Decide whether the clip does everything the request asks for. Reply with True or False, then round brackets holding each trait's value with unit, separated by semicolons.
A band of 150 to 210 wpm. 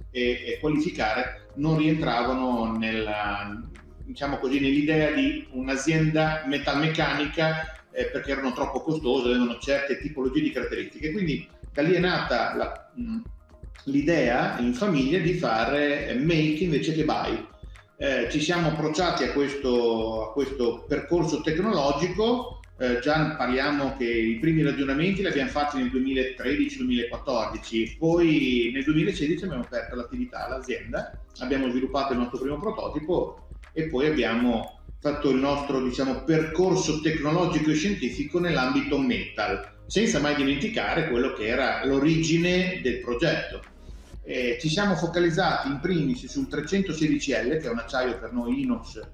False (135 wpm)